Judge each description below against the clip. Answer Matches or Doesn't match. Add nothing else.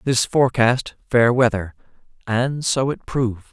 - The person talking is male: Matches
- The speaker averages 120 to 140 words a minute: Matches